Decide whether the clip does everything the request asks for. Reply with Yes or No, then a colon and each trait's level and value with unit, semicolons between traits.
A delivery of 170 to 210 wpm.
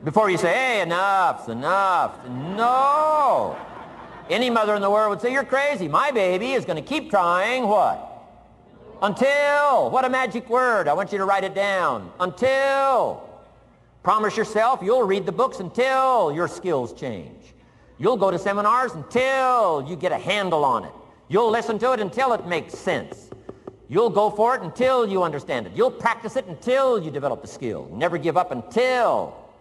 Yes: average, 175 wpm